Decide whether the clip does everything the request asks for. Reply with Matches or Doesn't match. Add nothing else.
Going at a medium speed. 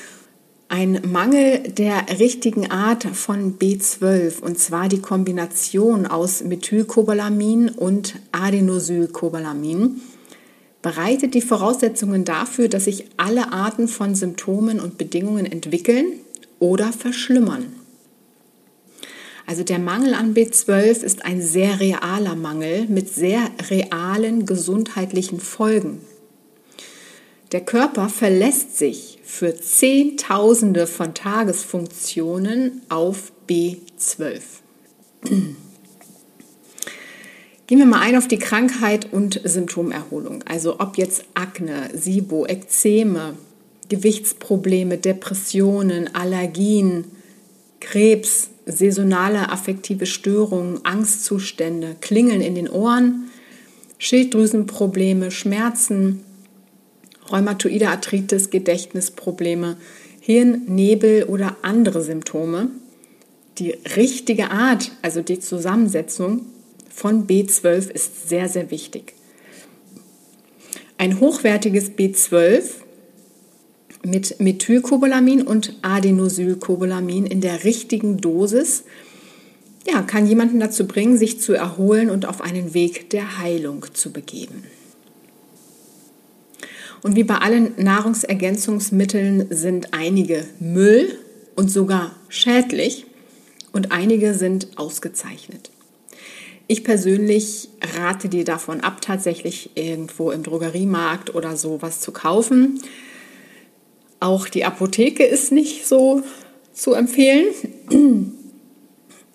Doesn't match